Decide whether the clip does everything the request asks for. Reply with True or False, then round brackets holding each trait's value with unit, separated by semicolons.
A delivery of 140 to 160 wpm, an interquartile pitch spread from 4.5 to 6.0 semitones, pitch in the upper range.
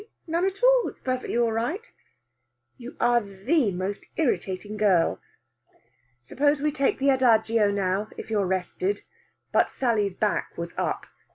True (145 wpm; 5.6 semitones; 225 Hz)